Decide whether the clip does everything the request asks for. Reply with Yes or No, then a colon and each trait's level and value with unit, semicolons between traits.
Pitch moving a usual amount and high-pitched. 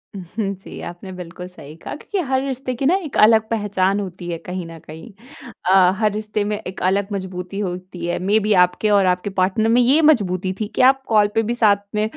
Yes: average, 3.3 semitones; high, 200 Hz